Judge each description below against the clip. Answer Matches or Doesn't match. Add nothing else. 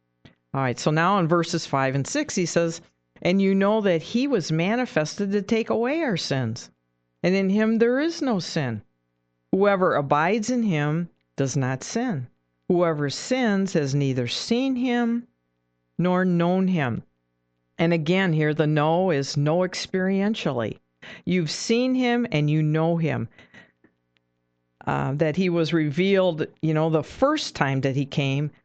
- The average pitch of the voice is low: Doesn't match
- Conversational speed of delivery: Matches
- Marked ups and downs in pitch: Matches